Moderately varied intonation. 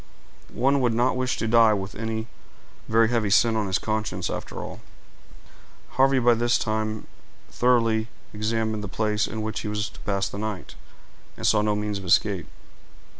No: narrow, 1.6 semitones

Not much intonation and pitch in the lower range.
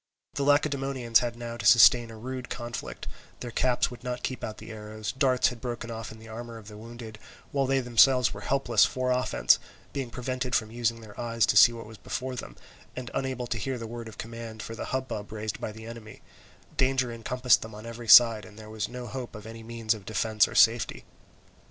Yes: narrow, 2.3 semitones; low, 115 Hz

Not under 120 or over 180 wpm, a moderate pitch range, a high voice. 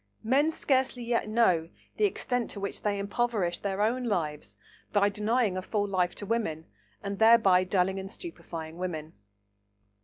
Yes: average, 155 wpm; average, 4.3 semitones; high, 200 Hz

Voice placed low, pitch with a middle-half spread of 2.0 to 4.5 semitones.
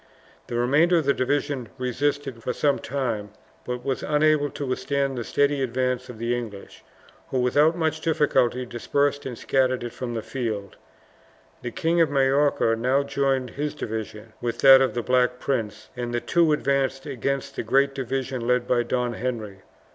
Yes: low, 130 Hz; average, 2.8 semitones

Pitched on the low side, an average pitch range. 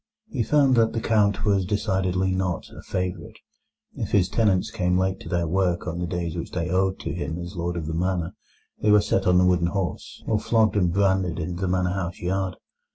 No: very low, 95 Hz; narrow, 2.2 semitones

